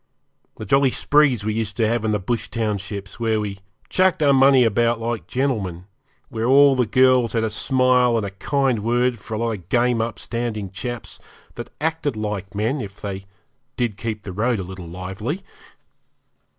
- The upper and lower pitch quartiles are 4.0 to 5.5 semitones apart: No, average, 3.6 semitones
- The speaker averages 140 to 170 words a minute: No, average, 180 wpm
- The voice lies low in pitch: Yes, low, 115 Hz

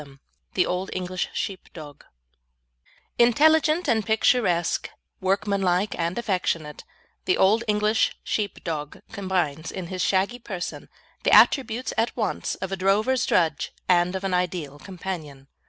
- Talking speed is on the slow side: Yes, slow, 130 wpm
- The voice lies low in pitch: No, high, 190 Hz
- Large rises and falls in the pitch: No, average, 3.9 semitones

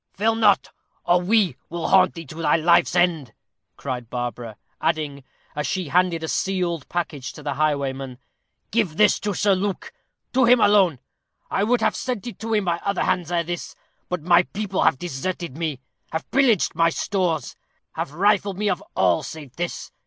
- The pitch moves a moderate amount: Yes, average, 4.8 semitones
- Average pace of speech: Yes, average, 180 wpm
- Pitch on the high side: No, medium, 175 Hz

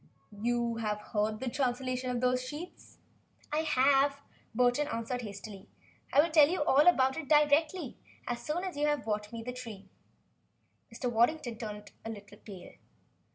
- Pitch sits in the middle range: No, very high, 250 Hz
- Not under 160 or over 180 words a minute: Yes, average, 165 wpm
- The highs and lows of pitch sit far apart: No, average, 4.6 semitones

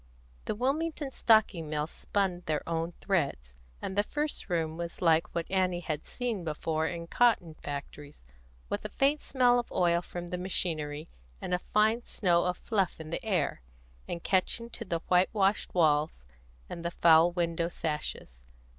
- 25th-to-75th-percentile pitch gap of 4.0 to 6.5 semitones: Yes, average, 4.3 semitones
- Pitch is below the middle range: No, medium, 175 Hz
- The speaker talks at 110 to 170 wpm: Yes, average, 165 wpm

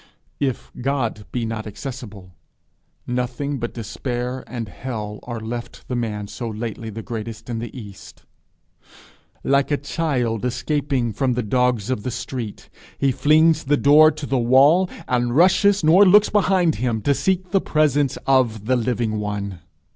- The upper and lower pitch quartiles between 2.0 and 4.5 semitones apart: Yes, average, 4.2 semitones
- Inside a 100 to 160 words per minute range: Yes, average, 155 wpm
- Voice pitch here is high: No, low, 125 Hz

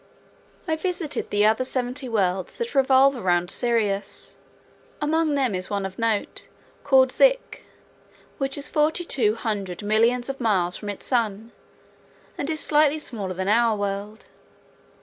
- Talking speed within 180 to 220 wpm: No, average, 145 wpm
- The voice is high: Yes, high, 235 Hz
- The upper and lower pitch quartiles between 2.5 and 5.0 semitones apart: No, wide, 5.5 semitones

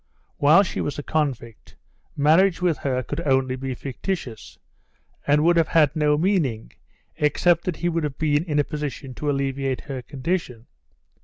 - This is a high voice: No, medium, 145 Hz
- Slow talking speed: No, average, 165 wpm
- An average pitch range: Yes, average, 3.7 semitones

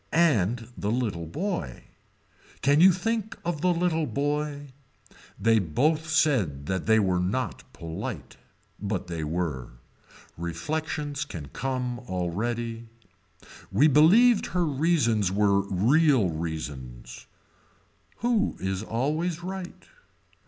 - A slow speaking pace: Yes, slow, 110 wpm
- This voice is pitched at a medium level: No, low, 120 Hz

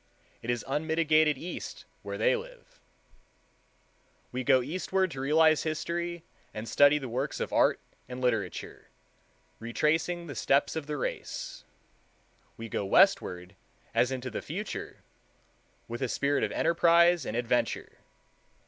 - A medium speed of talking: No, slow, 130 wpm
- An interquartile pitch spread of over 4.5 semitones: Yes, average, 5.2 semitones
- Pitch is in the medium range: Yes, medium, 150 Hz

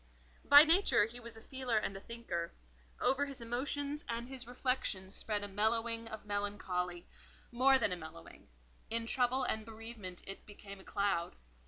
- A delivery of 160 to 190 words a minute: Yes, average, 165 wpm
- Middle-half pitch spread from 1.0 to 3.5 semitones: No, average, 3.9 semitones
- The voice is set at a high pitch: Yes, high, 225 Hz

